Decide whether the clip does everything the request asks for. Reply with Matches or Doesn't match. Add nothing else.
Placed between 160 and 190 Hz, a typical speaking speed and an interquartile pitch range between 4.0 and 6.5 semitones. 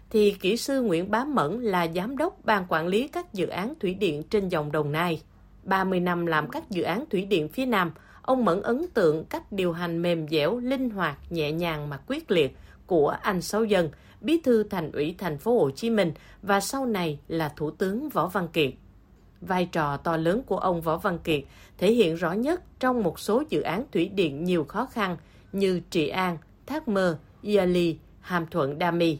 Matches